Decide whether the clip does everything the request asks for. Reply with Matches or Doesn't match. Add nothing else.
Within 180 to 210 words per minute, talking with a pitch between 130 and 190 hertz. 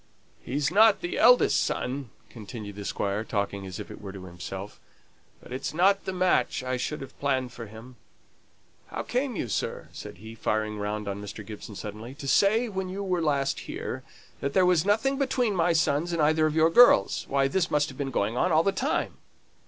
Matches